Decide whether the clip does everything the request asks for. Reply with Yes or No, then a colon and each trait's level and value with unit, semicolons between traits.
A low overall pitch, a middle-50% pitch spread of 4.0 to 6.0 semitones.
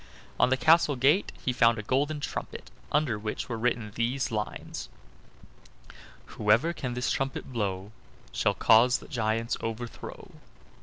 No: low, 120 Hz; average, 3.5 semitones